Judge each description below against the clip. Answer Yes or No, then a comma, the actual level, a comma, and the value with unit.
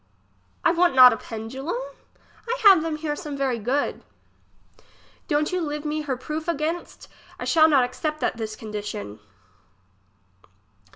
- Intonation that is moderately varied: Yes, average, 4.4 semitones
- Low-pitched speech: No, very high, 295 Hz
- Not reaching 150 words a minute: Yes, average, 140 wpm